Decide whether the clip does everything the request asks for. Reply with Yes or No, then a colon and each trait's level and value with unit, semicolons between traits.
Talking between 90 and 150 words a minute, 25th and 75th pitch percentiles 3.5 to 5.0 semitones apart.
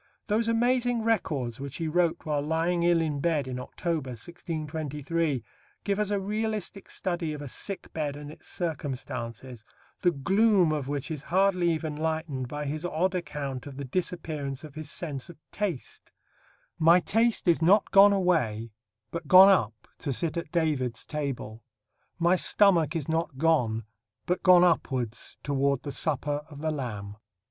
No: average, 160 wpm; average, 4.2 semitones